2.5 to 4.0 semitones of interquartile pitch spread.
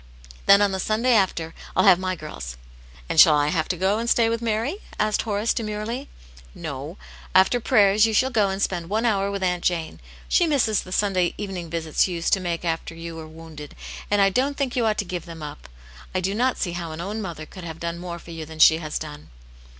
No: average, 4.5 semitones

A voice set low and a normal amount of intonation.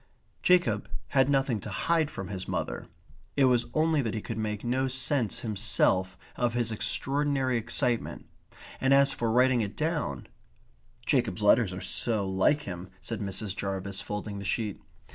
Yes: low, 115 Hz; average, 5.0 semitones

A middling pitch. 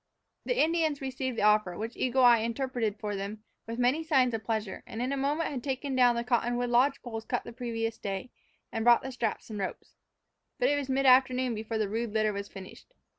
No: high, 240 Hz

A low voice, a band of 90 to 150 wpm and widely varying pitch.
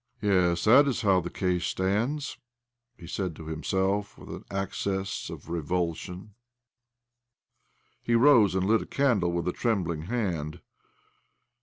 No: very low, 95 Hz; average, 140 wpm; average, 3.7 semitones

